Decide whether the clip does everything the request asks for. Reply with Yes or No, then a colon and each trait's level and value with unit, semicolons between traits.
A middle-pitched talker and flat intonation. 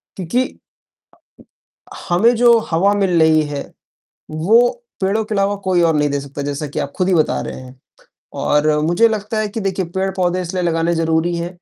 No: medium, 180 Hz; average, 3.9 semitones